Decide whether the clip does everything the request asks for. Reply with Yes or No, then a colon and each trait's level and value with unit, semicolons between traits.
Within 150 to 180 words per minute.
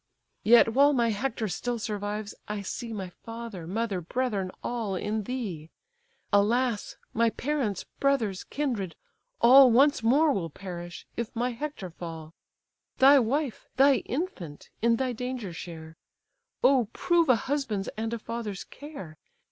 No: average, 140 wpm